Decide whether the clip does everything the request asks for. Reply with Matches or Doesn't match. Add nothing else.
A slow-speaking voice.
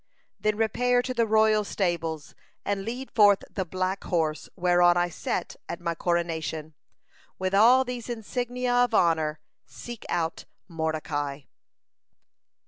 Matches